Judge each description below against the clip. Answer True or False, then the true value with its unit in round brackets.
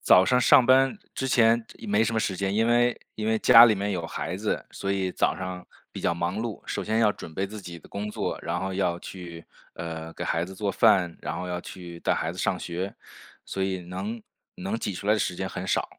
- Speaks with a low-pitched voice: True (95 Hz)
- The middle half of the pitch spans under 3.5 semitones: False (3.8 semitones)